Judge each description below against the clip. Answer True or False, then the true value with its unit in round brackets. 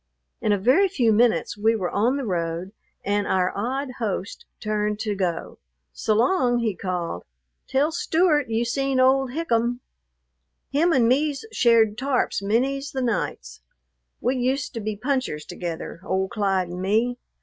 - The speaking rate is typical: True (150 wpm)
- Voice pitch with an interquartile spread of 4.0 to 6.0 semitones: True (4.9 semitones)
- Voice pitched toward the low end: False (230 Hz)